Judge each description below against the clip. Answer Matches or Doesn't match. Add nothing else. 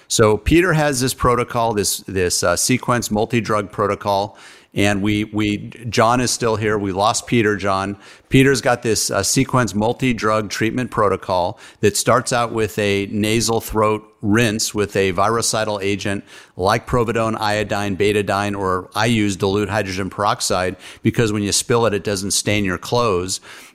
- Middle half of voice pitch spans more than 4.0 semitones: Doesn't match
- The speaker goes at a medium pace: Matches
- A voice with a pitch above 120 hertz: Doesn't match